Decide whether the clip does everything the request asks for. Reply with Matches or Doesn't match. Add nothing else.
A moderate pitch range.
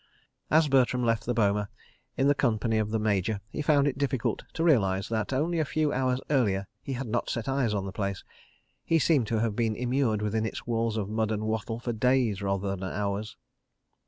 Matches